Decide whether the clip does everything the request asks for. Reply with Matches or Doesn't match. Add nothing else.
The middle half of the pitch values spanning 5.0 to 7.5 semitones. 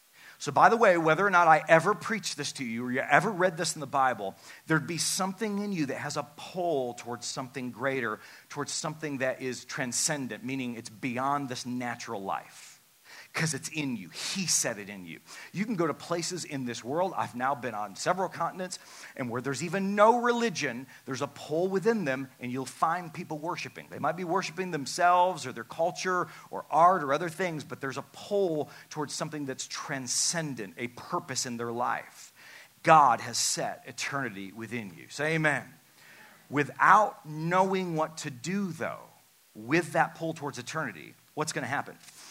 Matches